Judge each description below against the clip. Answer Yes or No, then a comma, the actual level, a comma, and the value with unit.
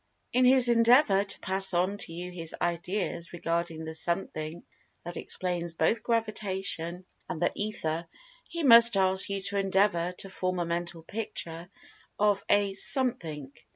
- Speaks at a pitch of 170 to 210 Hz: Yes, medium, 185 Hz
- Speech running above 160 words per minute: No, average, 150 wpm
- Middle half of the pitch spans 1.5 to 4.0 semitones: Yes, average, 3.4 semitones